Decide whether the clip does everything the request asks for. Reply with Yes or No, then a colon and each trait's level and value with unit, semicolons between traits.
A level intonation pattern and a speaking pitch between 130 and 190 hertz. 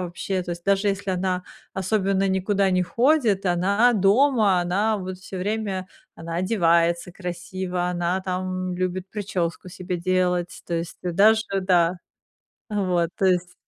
Yes: narrow, 1.8 semitones; medium, 185 Hz